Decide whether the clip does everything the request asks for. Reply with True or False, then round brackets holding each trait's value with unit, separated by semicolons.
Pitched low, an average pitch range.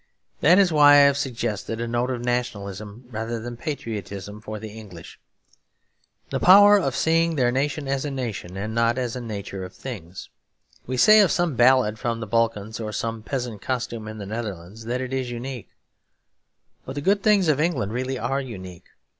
True (120 Hz; 3.9 semitones)